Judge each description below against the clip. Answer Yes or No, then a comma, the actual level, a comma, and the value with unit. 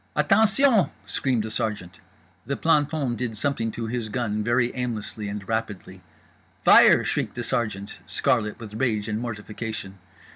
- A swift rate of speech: No, average, 140 wpm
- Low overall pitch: Yes, low, 115 Hz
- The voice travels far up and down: No, average, 3.5 semitones